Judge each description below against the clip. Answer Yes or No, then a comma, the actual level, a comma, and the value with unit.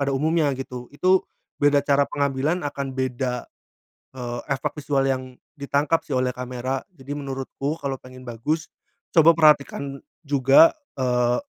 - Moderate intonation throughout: No, narrow, 2.2 semitones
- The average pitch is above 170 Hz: No, low, 135 Hz